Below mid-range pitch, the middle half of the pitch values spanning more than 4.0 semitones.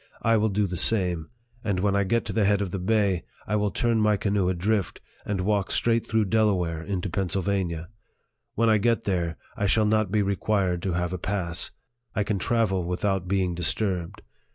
No: low, 100 Hz; average, 2.9 semitones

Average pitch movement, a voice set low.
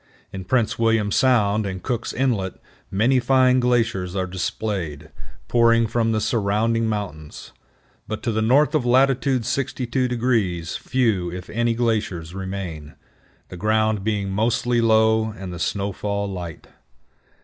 Yes: average, 3.7 semitones; low, 110 Hz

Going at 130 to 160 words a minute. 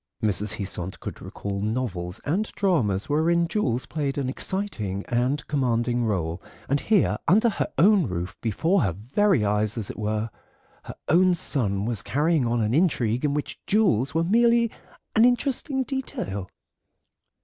Yes: average, 150 wpm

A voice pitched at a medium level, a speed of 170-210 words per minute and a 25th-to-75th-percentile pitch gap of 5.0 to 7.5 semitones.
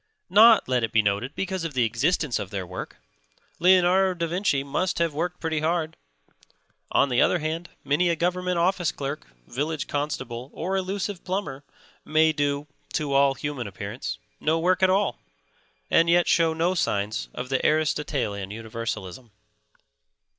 No: medium, 155 Hz; average, 155 wpm; wide, 5.6 semitones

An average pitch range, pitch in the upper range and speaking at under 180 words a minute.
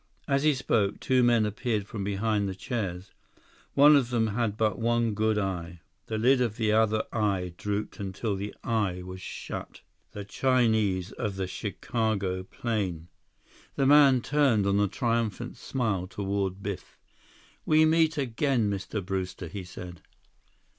No: average, 3.6 semitones; low, 105 Hz; average, 150 wpm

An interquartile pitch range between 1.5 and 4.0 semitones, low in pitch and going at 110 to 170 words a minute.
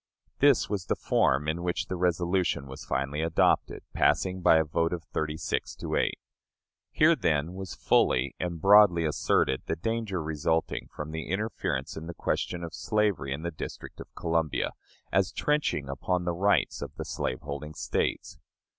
Yes: average, 3.4 semitones; very low, 85 Hz; average, 165 wpm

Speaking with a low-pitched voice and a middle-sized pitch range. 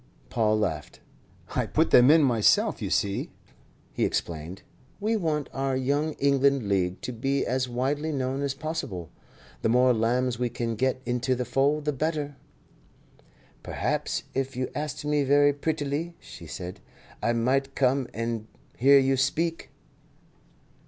Yes: low, 130 Hz; average, 3.4 semitones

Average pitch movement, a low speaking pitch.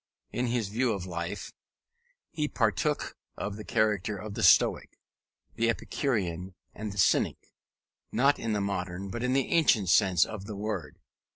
Yes: average, 3.7 semitones; low, 105 Hz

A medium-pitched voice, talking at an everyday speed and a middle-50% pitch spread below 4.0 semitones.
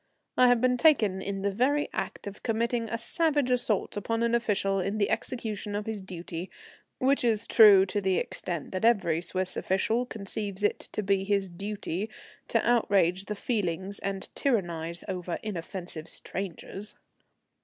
No: high, 200 Hz; average, 160 wpm; average, 3.4 semitones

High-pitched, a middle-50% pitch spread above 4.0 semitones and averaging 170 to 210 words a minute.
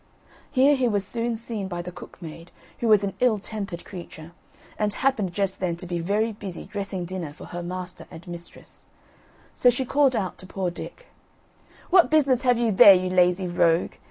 Yes: high, 195 Hz; average, 4.8 semitones; average, 190 wpm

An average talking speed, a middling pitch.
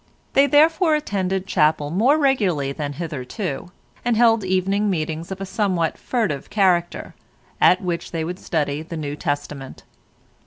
Yes: average, 145 wpm; medium, 180 Hz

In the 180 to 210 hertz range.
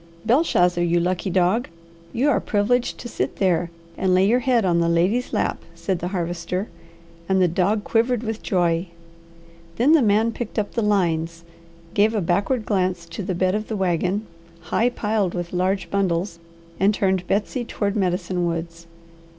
Yes: high, 190 Hz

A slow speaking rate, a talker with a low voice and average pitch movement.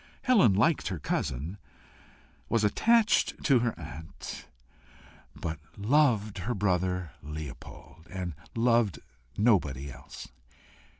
No: slow, 100 wpm; very low, 95 Hz; wide, 6.4 semitones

